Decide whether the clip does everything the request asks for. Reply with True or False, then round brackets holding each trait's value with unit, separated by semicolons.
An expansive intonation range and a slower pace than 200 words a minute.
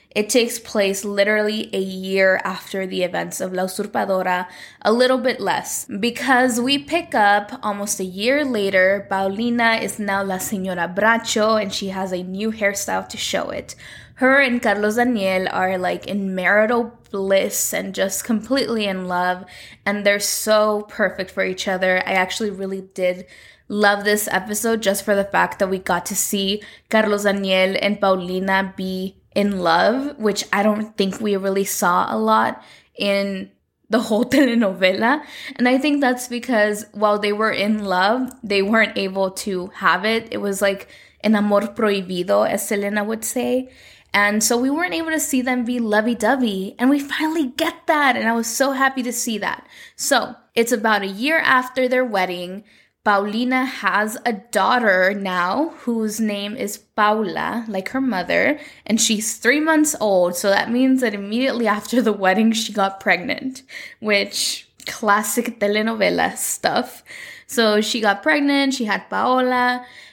False (3.8 semitones; 165 wpm)